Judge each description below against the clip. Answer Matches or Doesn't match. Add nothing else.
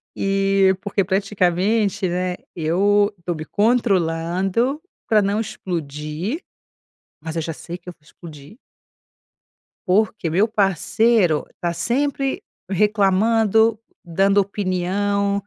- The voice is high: Matches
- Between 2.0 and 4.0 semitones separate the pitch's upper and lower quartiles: Matches